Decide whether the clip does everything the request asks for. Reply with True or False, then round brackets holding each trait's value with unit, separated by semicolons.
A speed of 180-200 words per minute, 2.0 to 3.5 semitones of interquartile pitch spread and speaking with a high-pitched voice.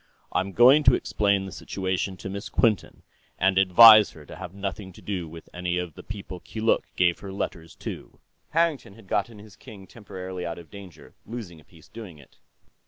False (190 wpm; 3.2 semitones; 95 Hz)